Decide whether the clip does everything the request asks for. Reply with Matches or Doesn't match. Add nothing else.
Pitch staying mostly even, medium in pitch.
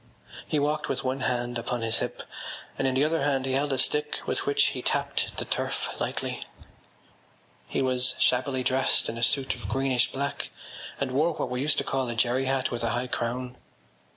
Doesn't match